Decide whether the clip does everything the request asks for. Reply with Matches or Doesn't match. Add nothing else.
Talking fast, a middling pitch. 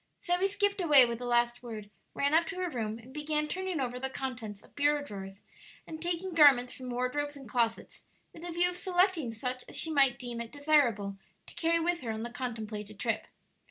Doesn't match